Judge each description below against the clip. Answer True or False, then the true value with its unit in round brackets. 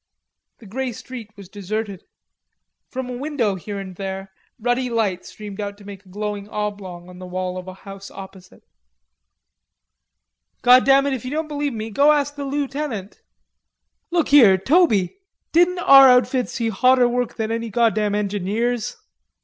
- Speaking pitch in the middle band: False (220 Hz)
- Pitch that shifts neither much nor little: True (4.8 semitones)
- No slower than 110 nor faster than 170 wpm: True (160 wpm)